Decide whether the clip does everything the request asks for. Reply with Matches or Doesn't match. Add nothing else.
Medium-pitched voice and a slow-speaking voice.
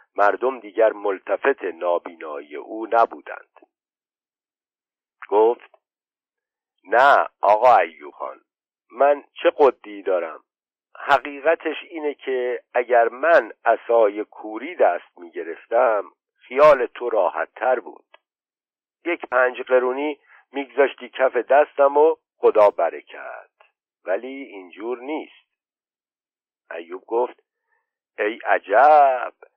Matches